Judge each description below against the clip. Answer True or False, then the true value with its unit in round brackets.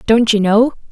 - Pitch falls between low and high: False (225 Hz)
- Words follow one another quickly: False (195 wpm)